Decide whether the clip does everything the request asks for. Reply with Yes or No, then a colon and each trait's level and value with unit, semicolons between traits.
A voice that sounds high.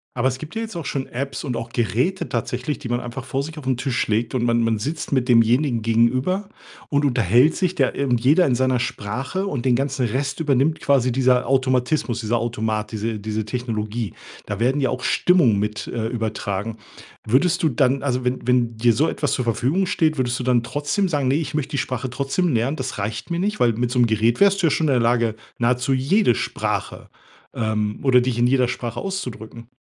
No: low, 125 Hz